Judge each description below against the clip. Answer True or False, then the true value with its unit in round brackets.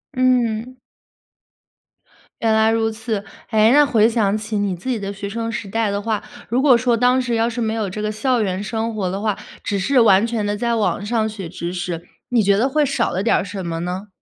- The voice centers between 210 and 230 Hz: True (220 Hz)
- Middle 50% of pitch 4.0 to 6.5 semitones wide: False (2.7 semitones)